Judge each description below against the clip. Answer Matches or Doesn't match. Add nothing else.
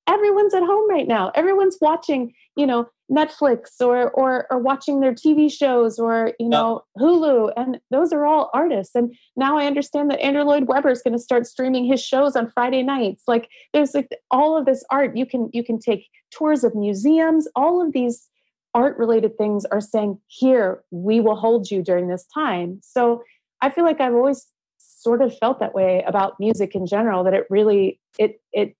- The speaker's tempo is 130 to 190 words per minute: Doesn't match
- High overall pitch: Matches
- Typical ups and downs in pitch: Matches